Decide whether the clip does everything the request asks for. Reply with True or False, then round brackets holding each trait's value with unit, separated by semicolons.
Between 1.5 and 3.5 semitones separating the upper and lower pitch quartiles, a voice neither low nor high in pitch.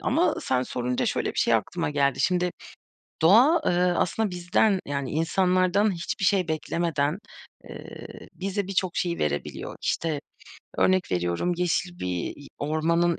False (4.2 semitones; 175 Hz)